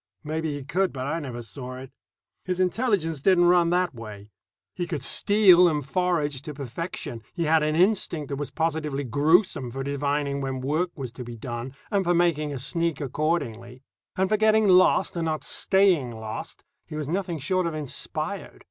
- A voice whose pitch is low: No, medium, 155 Hz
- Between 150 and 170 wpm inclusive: No, average, 185 wpm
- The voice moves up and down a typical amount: Yes, average, 4.7 semitones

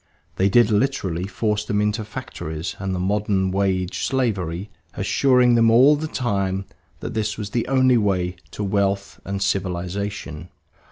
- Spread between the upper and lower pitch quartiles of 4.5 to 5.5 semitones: No, average, 3.2 semitones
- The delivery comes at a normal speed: Yes, average, 150 wpm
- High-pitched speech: No, low, 100 Hz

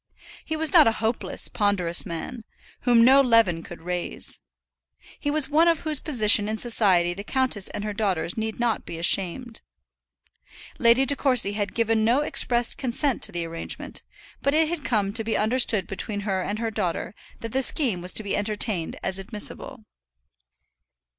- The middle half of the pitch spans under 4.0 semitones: No, average, 4.5 semitones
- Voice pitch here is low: No, high, 220 Hz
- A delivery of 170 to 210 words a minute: Yes, average, 175 wpm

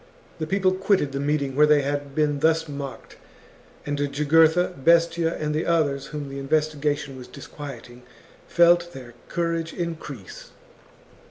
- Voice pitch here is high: No, medium, 150 Hz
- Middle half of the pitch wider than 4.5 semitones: No, average, 2.8 semitones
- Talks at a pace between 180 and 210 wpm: No, average, 145 wpm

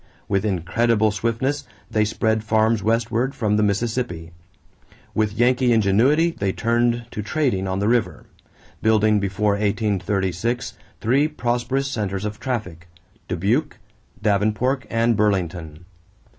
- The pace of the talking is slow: Yes, slow, 115 wpm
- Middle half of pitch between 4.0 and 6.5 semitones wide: No, average, 3.1 semitones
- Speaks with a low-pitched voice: Yes, low, 110 Hz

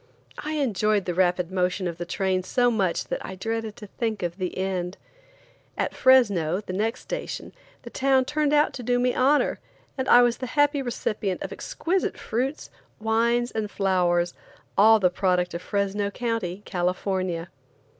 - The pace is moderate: Yes, average, 165 wpm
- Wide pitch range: No, average, 5.0 semitones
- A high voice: Yes, high, 205 Hz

